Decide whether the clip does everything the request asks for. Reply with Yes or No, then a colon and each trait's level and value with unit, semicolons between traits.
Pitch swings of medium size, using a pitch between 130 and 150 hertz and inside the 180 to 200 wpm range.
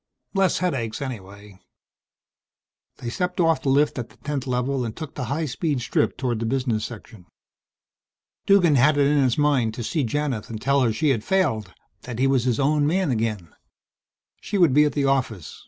Yes: average, 4.5 semitones; low, 135 Hz; average, 190 wpm